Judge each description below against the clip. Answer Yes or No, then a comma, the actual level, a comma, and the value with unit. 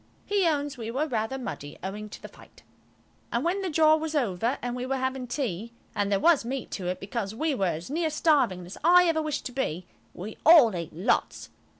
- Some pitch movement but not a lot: No, wide, 7.2 semitones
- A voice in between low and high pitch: No, very high, 250 Hz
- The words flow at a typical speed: No, fast, 210 wpm